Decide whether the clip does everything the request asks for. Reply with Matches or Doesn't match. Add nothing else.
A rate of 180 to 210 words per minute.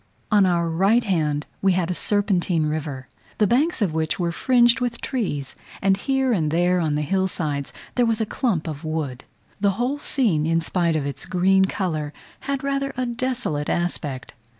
Matches